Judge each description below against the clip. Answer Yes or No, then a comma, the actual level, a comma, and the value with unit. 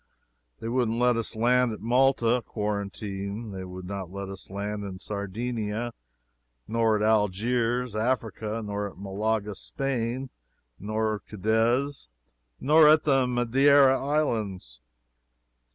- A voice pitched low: Yes, low, 110 Hz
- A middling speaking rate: No, slow, 120 wpm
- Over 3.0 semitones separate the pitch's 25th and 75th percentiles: Yes, average, 3.5 semitones